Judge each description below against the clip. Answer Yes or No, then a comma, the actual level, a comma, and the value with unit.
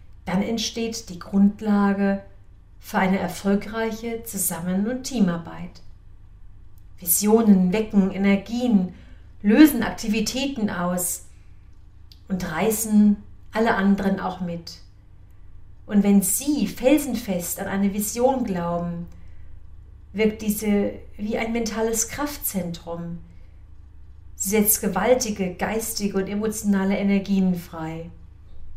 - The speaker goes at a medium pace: No, slow, 90 wpm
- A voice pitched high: Yes, high, 195 Hz